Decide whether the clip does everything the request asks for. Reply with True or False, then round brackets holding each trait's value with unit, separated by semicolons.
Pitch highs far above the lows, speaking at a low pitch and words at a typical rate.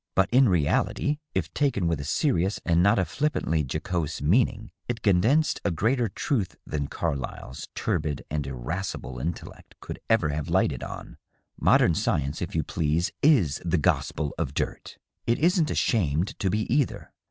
True (7.0 semitones; 90 Hz; 160 wpm)